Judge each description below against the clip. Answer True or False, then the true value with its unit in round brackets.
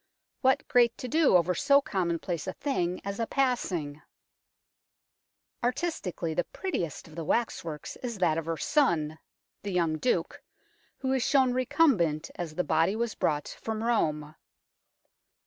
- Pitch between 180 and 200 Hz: True (185 Hz)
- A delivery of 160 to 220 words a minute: False (145 wpm)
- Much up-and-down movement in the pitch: True (7.5 semitones)